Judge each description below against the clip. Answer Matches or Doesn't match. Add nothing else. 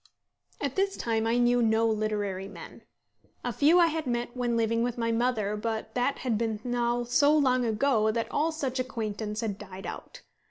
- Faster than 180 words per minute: Matches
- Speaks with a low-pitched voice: Doesn't match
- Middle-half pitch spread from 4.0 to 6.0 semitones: Doesn't match